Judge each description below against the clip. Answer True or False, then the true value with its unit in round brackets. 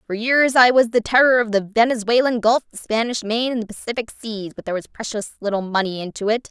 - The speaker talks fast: True (230 wpm)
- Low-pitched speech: False (225 Hz)